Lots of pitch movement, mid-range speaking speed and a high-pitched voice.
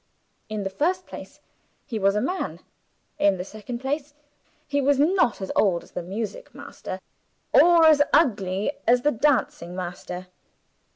Yes: wide, 7.3 semitones; average, 155 wpm; high, 230 Hz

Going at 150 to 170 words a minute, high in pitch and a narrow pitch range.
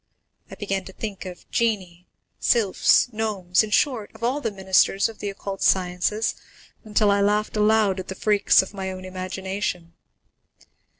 Yes: average, 160 wpm; high, 200 Hz; narrow, 2.3 semitones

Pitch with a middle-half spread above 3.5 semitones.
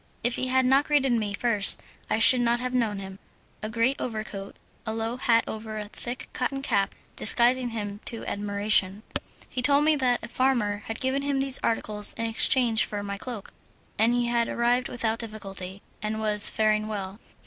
No: average, 3.1 semitones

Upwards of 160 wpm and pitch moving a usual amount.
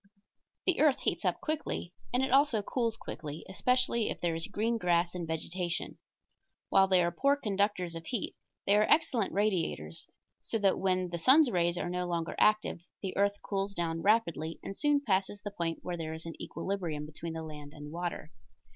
Yes: average, 190 wpm; average, 4.3 semitones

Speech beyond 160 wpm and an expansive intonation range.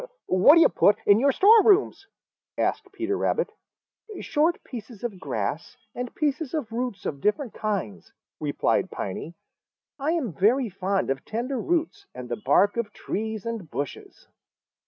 No: average, 150 wpm; wide, 8.2 semitones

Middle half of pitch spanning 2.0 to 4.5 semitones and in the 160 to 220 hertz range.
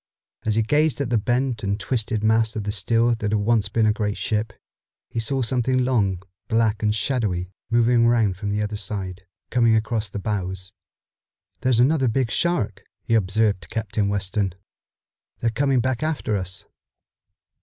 No: average, 2.8 semitones; low, 110 Hz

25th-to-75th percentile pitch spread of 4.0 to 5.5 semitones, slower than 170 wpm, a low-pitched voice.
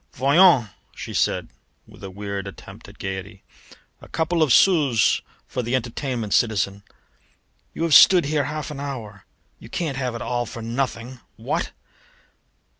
Yes: average, 5.2 semitones; average, 150 wpm; low, 125 Hz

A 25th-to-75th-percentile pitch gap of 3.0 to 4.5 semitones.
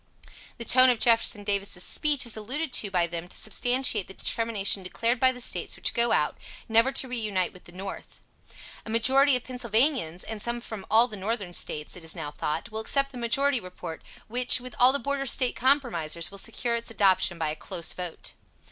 No: average, 5.0 semitones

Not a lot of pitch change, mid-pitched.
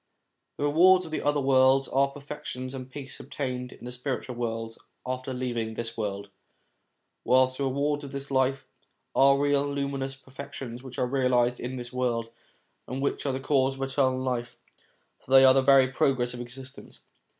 No: narrow, 1.7 semitones; low, 130 Hz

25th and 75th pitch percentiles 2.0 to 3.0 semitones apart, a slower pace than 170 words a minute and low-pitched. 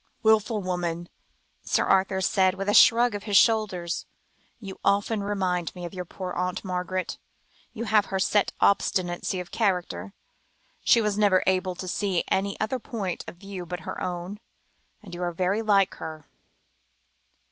No: narrow, 2.4 semitones; average, 160 wpm; high, 190 Hz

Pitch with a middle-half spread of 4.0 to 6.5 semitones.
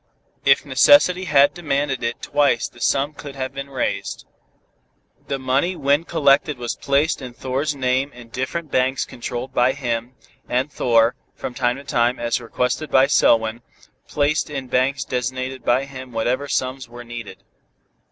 No: narrow, 2.5 semitones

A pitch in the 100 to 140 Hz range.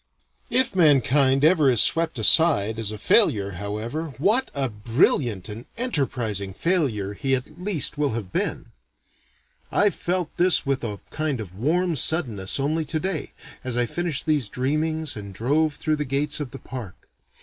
Yes: low, 135 Hz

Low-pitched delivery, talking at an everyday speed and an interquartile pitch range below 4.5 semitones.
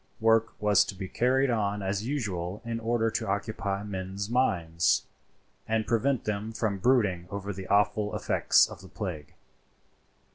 Yes: low, 105 Hz; average, 150 wpm; average, 2.7 semitones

